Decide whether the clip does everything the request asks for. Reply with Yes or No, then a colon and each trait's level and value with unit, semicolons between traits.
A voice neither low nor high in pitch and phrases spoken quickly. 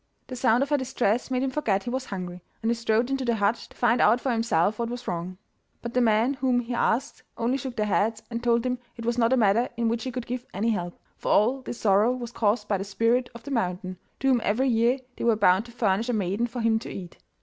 No: high, 235 Hz; fast, 265 wpm